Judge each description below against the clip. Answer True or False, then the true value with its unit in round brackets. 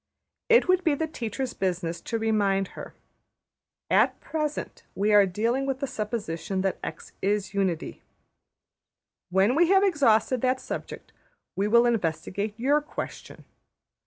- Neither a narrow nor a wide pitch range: False (5.7 semitones)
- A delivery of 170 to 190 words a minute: False (135 wpm)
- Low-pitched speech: False (220 Hz)